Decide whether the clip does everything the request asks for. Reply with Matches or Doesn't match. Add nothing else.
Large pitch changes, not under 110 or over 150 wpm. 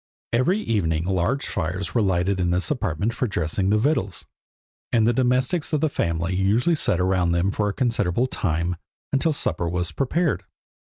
Doesn't match